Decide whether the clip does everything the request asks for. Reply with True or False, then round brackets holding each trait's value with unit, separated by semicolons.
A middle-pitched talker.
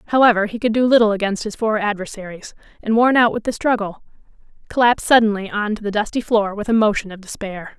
False (215 Hz)